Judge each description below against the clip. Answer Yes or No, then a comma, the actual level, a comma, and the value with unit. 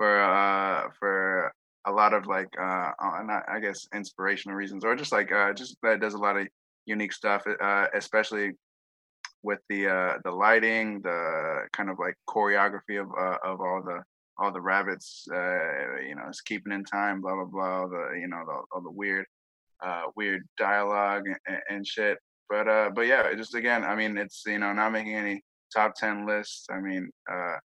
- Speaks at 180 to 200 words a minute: Yes, average, 190 wpm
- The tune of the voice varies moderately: No, narrow, 1.6 semitones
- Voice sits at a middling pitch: No, low, 100 Hz